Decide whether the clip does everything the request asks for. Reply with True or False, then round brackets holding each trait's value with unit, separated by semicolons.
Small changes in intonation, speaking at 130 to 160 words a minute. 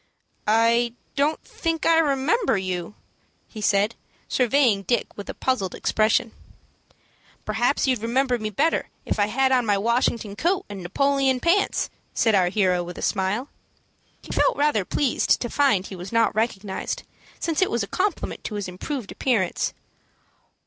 False (5.3 semitones; 155 wpm)